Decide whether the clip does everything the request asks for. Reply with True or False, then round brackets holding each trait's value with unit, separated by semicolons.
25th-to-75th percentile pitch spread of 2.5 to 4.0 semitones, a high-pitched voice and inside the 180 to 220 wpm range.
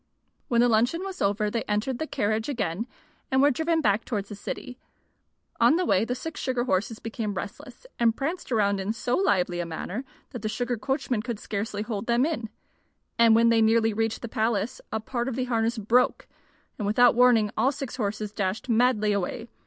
True (3.0 semitones; 230 Hz; 200 wpm)